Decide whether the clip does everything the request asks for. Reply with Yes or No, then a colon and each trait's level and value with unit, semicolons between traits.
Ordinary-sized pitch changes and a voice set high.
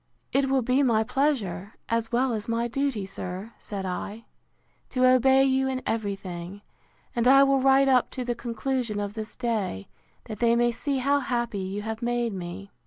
Yes: average, 4.1 semitones; high, 235 Hz